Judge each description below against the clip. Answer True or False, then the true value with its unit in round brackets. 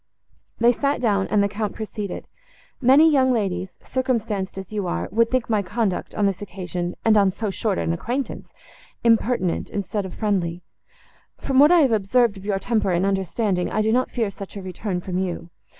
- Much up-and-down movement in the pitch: False (3.6 semitones)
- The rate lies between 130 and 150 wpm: False (190 wpm)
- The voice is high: True (205 Hz)